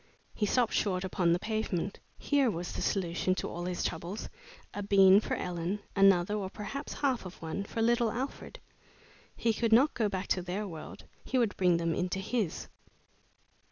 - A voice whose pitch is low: No, high, 195 Hz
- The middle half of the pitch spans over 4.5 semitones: No, average, 3.9 semitones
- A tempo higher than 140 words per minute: Yes, average, 180 wpm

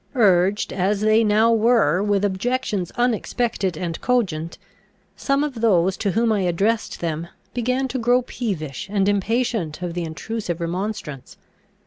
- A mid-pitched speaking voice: No, high, 205 Hz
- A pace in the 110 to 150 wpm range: Yes, average, 140 wpm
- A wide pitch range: No, average, 4.6 semitones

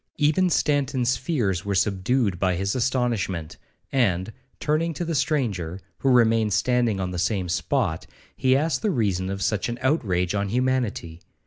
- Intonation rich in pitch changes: Yes, wide, 5.8 semitones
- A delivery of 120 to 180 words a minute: Yes, average, 155 wpm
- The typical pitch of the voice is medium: No, low, 115 Hz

